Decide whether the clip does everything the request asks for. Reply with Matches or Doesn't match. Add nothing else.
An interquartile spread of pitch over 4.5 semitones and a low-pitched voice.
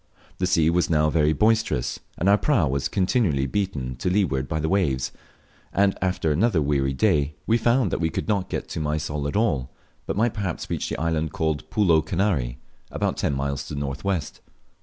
Matches